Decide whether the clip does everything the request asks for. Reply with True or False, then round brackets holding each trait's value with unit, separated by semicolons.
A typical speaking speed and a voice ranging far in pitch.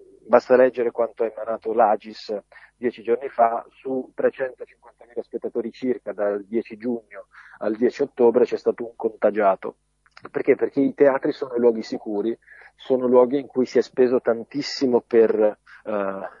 False (145 wpm; 3.7 semitones)